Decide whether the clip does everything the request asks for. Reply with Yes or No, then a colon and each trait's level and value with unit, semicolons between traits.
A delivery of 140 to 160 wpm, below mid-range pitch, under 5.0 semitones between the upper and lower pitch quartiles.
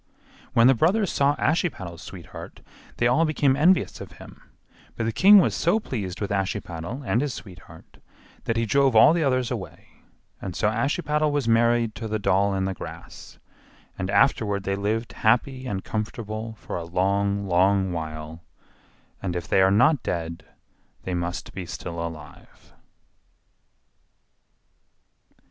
No: average, 150 wpm; low, 110 Hz; wide, 5.5 semitones